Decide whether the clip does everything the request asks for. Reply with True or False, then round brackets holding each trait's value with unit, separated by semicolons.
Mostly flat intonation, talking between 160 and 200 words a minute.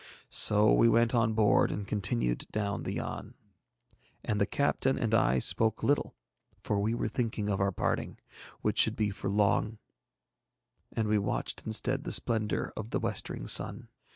True (2.2 semitones; 165 wpm)